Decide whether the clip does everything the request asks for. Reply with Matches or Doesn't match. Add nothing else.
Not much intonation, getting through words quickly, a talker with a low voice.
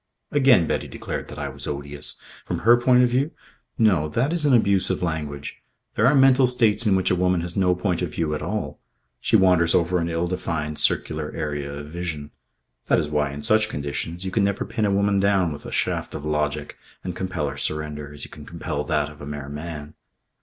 Doesn't match